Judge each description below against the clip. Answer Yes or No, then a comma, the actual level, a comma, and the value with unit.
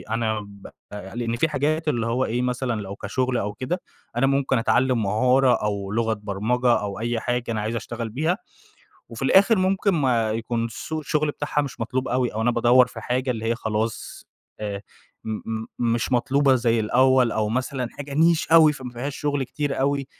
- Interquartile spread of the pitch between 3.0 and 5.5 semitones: Yes, average, 3.4 semitones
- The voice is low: Yes, low, 125 Hz